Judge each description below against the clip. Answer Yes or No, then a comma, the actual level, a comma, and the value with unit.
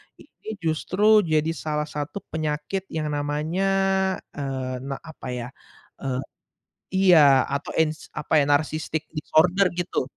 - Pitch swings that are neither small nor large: No, narrow, 2.1 semitones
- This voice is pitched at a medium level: Yes, medium, 155 Hz